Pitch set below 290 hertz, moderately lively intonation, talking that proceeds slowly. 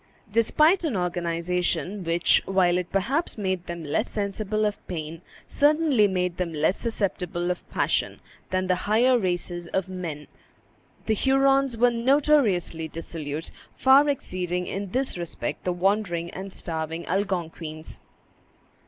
Yes: medium, 185 Hz; average, 4.5 semitones; slow, 130 wpm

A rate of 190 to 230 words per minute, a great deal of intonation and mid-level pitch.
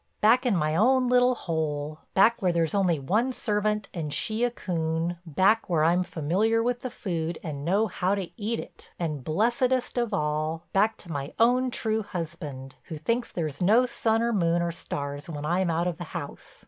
Yes: average, 195 wpm; wide, 5.9 semitones; medium, 180 Hz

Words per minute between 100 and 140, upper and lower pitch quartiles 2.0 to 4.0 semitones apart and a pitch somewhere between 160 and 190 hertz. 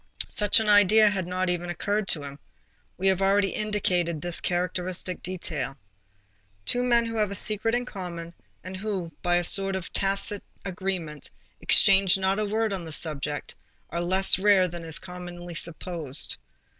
No: average, 165 wpm; average, 2.7 semitones; medium, 185 Hz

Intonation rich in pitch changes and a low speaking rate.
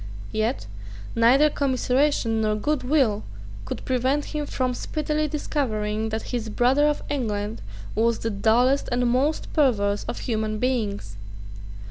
No: average, 4.4 semitones; slow, 130 wpm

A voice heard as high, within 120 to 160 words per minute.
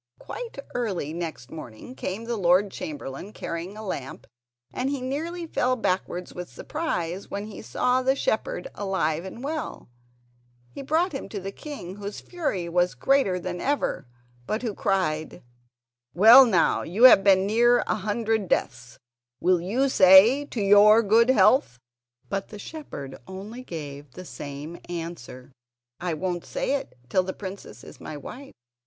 Yes: high, 195 Hz; average, 155 wpm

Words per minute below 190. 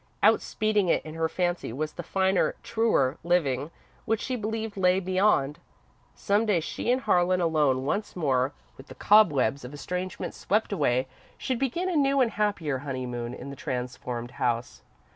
Yes: average, 160 wpm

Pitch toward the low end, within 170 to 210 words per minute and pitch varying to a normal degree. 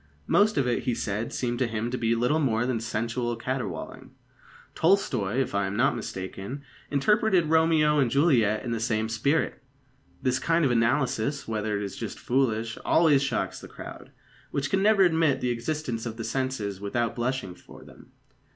Yes: low, 125 Hz; average, 180 wpm; average, 4.2 semitones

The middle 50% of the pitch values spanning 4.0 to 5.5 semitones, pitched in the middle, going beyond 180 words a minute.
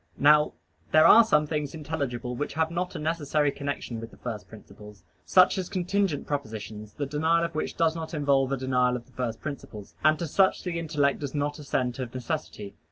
Yes: average, 4.3 semitones; medium, 145 Hz; average, 200 wpm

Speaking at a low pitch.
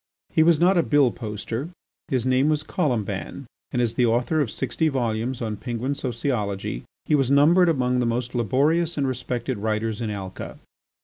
Yes: low, 125 Hz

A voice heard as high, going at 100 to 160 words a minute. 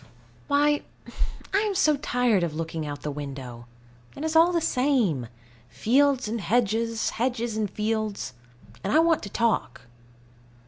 Yes: high, 225 Hz; average, 150 wpm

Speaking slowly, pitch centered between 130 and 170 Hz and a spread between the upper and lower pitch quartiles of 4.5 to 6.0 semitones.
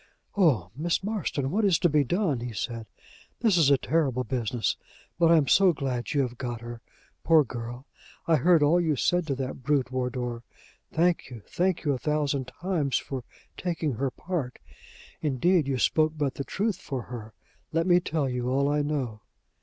No: average, 185 wpm; medium, 140 Hz; average, 4.8 semitones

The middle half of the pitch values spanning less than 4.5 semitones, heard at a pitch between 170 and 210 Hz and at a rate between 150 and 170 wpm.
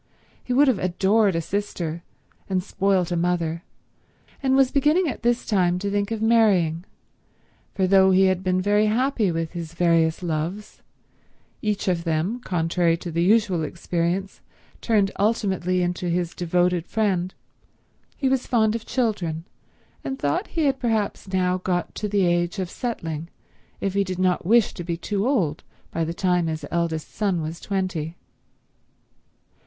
Yes: average, 3.7 semitones; medium, 185 Hz; average, 160 wpm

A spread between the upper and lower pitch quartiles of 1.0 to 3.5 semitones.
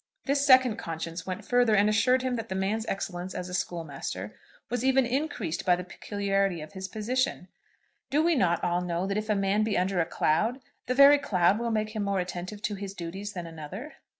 No: average, 4.8 semitones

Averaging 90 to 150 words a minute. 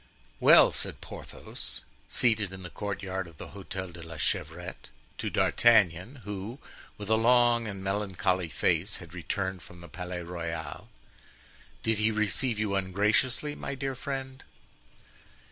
Yes: average, 140 wpm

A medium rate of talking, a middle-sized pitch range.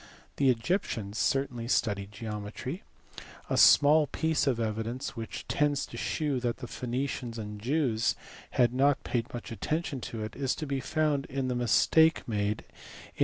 Yes: average, 160 wpm; average, 4.0 semitones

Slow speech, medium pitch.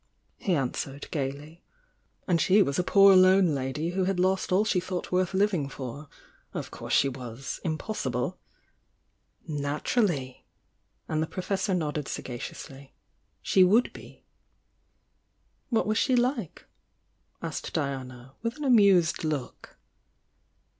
Yes: slow, 125 wpm; medium, 170 Hz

